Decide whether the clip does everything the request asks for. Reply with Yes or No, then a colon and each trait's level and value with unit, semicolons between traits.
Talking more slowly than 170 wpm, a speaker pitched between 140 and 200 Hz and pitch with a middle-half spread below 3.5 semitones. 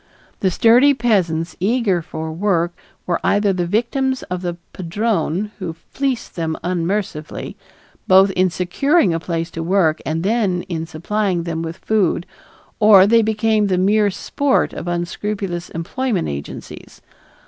No: average, 140 wpm; medium, 185 Hz; average, 4.2 semitones